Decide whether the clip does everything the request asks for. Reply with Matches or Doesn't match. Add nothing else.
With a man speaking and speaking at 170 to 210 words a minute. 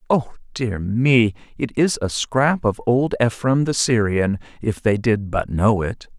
Matches